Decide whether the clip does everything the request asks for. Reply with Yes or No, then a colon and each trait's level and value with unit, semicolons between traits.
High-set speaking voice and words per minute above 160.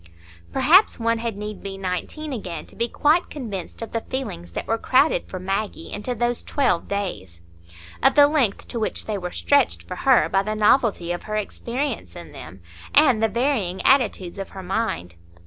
Yes: high, 215 Hz; average, 185 wpm